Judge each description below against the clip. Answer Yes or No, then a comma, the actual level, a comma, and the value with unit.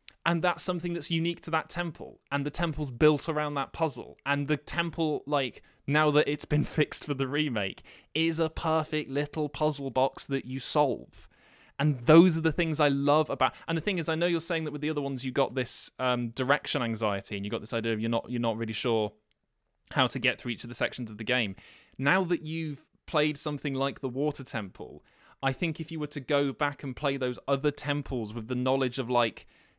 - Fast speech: Yes, fast, 230 wpm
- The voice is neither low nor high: Yes, medium, 145 Hz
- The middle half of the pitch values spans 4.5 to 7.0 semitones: No, average, 3.5 semitones